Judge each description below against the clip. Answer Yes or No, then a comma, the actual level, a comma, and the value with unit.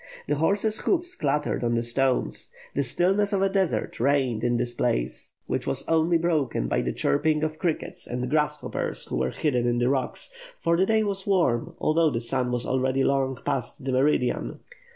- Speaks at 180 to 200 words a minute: Yes, average, 190 wpm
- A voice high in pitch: No, medium, 140 Hz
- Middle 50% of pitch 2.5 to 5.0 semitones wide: No, wide, 5.4 semitones